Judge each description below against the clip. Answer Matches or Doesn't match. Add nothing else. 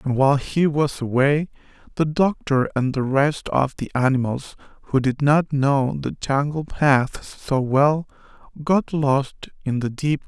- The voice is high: Doesn't match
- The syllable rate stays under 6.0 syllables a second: Matches